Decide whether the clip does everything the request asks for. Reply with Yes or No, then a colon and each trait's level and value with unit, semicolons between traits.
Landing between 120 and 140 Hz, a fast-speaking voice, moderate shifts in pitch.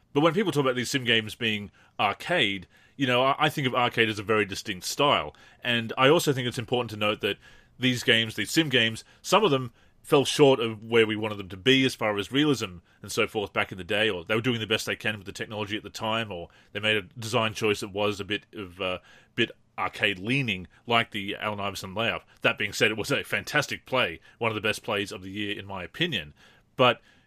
No: low, 110 Hz; fast, 245 wpm; average, 3.4 semitones